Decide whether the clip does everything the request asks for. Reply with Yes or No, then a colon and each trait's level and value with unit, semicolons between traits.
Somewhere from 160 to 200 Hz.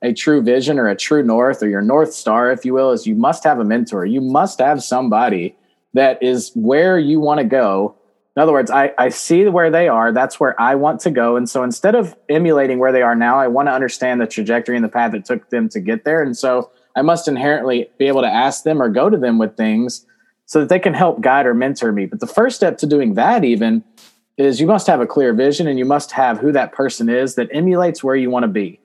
No: low, 135 Hz